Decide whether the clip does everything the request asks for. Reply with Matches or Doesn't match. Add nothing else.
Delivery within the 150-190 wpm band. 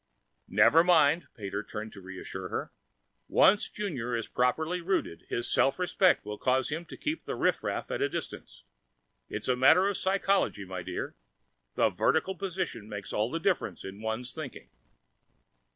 Matches